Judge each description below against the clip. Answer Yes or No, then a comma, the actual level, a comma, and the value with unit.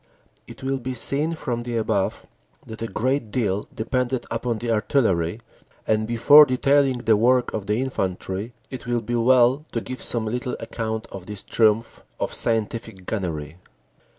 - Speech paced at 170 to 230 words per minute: No, average, 160 wpm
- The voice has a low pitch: Yes, low, 115 Hz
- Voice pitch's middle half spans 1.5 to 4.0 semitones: Yes, average, 2.9 semitones